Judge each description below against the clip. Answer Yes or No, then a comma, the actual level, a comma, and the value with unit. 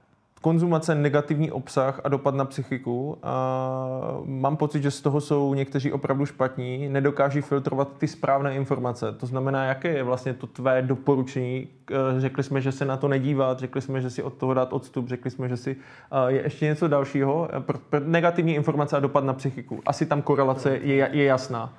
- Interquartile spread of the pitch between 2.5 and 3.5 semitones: No, narrow, 1.7 semitones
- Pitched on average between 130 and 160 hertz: Yes, low, 135 Hz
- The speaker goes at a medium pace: No, fast, 175 wpm